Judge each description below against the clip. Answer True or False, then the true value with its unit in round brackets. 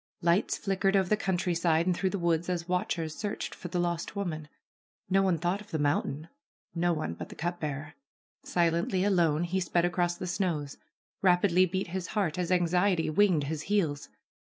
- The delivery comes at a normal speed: True (185 wpm)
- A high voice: False (175 Hz)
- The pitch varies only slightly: True (2.3 semitones)